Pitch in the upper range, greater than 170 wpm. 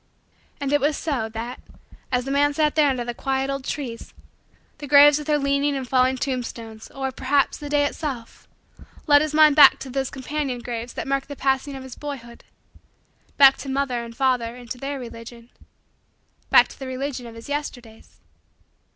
Yes: very high, 270 Hz; average, 185 wpm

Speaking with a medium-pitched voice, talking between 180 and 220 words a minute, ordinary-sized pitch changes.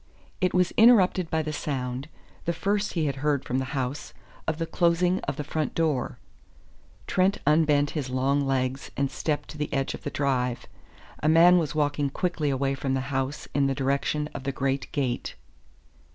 Yes: medium, 145 Hz; average, 185 wpm; average, 3.2 semitones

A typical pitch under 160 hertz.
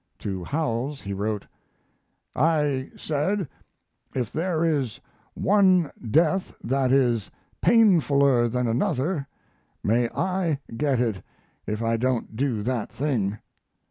Yes: low, 135 Hz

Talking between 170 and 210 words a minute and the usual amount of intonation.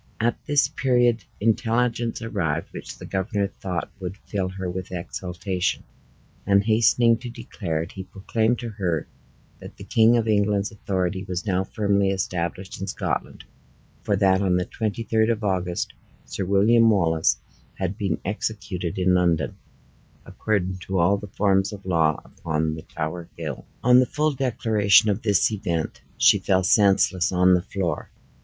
No: average, 160 wpm; average, 3.4 semitones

